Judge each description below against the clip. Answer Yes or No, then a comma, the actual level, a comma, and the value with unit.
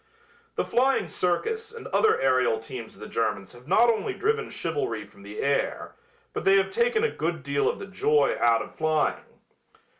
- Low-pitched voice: No, medium, 180 Hz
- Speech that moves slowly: No, average, 185 wpm